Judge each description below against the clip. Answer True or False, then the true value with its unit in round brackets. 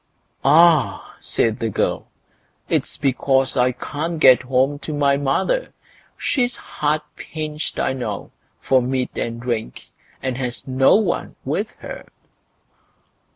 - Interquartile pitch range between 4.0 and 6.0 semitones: False (3.2 semitones)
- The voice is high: False (135 Hz)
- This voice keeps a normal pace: False (125 wpm)